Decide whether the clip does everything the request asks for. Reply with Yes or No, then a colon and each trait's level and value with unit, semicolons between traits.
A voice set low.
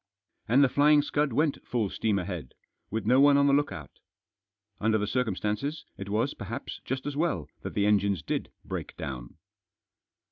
Yes: low, 115 Hz